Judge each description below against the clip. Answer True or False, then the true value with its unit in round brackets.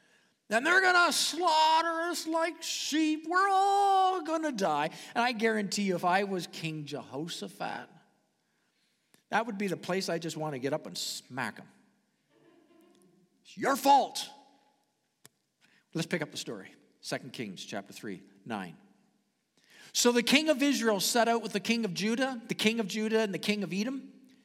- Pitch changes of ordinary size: False (8.4 semitones)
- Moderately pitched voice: False (230 Hz)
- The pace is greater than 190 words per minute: False (170 wpm)